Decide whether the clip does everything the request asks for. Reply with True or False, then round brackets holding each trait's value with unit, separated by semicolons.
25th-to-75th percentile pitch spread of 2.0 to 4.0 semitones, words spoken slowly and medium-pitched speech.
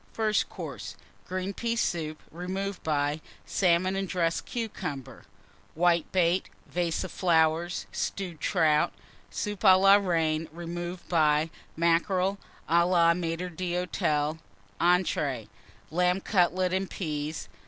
True (2.5 semitones; 110 wpm; 175 Hz)